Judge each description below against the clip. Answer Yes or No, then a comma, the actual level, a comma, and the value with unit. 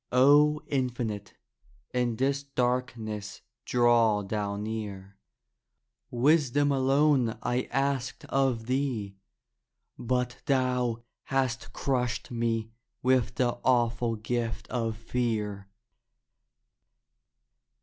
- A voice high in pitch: No, low, 120 Hz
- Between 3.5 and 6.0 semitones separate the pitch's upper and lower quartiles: No, average, 2.7 semitones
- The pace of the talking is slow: Yes, slow, 85 wpm